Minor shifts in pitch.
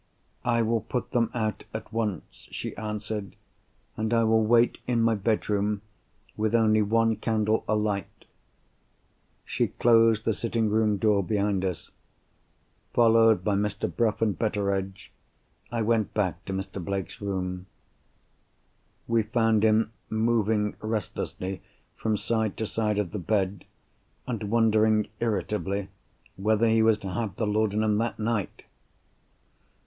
Yes: narrow, 1.8 semitones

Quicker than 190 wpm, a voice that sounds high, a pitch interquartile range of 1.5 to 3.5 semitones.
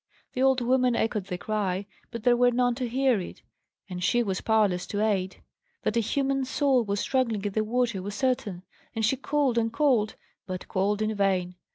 No: average, 200 wpm; high, 225 Hz; average, 4.0 semitones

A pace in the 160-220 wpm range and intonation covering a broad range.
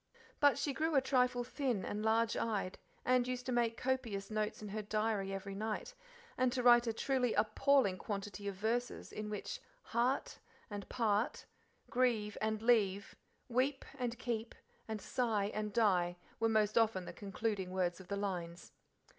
No: average, 165 wpm; average, 3.4 semitones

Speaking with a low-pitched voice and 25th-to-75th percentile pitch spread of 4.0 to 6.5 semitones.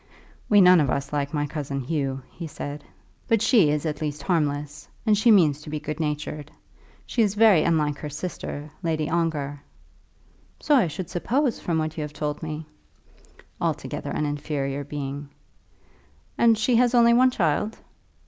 No: medium, 155 Hz; average, 4.6 semitones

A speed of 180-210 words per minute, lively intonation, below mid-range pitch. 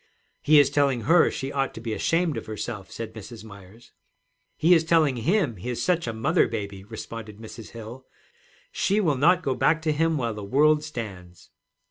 Yes: average, 190 wpm; wide, 5.8 semitones; low, 125 Hz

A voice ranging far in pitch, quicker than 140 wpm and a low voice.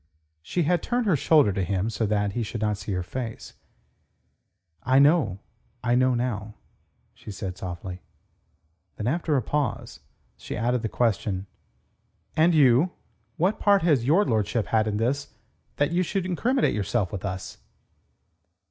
Yes: wide, 7.0 semitones; average, 155 wpm; low, 120 Hz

